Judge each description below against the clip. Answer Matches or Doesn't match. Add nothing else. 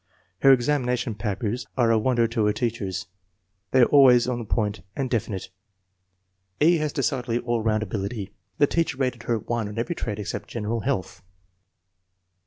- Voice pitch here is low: Matches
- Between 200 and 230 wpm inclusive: Doesn't match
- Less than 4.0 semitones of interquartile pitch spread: Matches